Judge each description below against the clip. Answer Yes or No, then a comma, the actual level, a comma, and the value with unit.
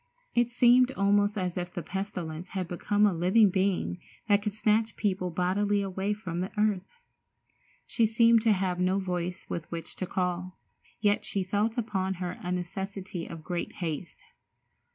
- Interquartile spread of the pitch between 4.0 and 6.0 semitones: No, average, 2.7 semitones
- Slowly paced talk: No, average, 165 wpm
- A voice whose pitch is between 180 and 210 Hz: Yes, high, 190 Hz